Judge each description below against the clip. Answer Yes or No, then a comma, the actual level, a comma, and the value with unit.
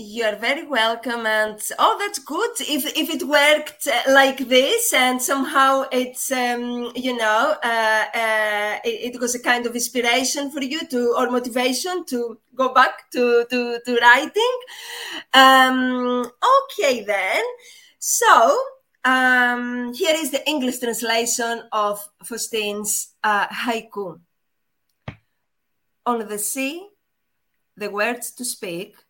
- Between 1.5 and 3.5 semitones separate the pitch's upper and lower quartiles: Yes, average, 3.2 semitones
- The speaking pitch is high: Yes, high, 245 Hz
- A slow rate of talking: Yes, slow, 130 wpm